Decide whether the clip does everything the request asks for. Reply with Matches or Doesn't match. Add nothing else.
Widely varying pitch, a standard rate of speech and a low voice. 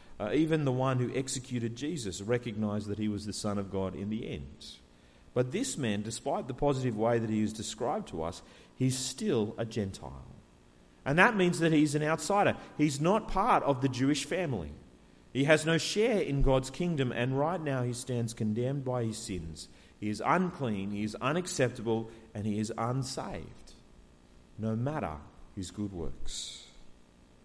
Matches